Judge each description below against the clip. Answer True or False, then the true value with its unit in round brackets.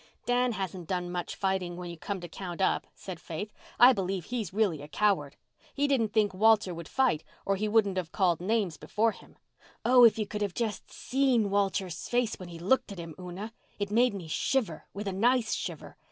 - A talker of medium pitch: False (200 Hz)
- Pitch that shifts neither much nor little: True (4.0 semitones)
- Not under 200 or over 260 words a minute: True (205 wpm)